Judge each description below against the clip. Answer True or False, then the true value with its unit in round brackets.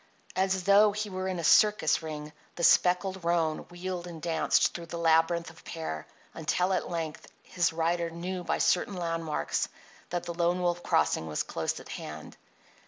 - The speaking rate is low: False (170 wpm)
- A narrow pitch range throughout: True (2.0 semitones)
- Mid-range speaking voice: True (170 Hz)